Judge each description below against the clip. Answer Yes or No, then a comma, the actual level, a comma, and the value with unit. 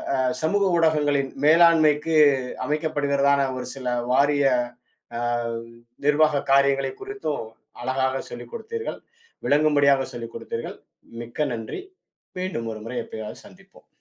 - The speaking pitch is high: No, medium, 140 Hz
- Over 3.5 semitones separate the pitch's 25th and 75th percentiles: No, average, 3.1 semitones